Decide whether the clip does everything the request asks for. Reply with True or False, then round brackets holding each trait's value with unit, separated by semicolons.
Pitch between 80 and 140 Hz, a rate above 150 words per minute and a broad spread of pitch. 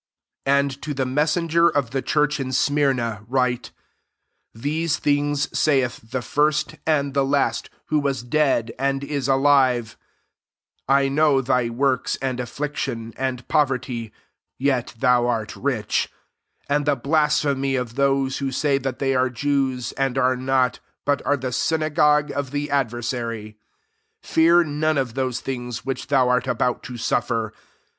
False (135 Hz; 160 wpm; 2.5 semitones)